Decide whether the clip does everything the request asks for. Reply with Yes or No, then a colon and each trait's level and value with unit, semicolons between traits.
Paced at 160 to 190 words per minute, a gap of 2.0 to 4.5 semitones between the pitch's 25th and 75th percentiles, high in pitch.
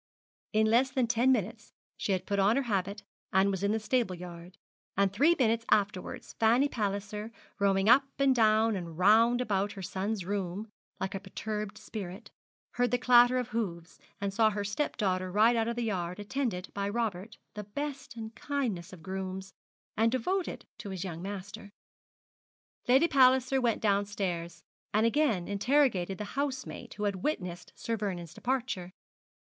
Yes: average, 165 wpm; average, 3.9 semitones; high, 210 Hz